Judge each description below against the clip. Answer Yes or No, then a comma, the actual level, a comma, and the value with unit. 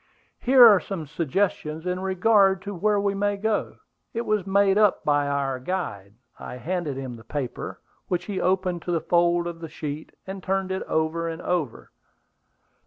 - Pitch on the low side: No, medium, 180 Hz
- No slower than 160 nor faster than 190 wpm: Yes, average, 180 wpm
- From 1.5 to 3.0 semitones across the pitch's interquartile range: No, average, 4.0 semitones